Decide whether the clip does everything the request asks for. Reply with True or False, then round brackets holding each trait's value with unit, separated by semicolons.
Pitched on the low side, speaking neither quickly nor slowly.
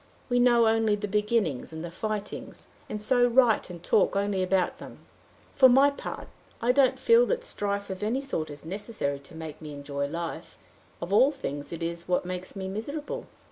False (200 Hz; 190 wpm)